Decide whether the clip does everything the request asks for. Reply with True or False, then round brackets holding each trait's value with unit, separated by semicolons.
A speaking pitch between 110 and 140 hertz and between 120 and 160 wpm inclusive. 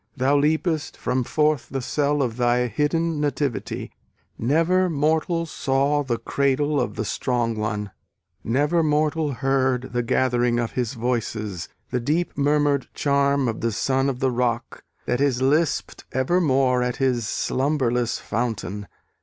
True (135 Hz; 140 wpm)